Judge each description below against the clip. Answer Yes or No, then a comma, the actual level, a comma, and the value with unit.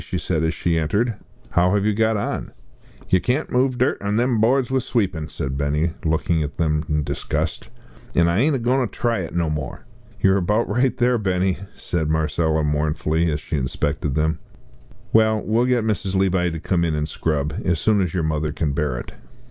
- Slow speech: No, fast, 205 wpm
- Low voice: Yes, very low, 85 Hz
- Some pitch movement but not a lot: No, wide, 6.1 semitones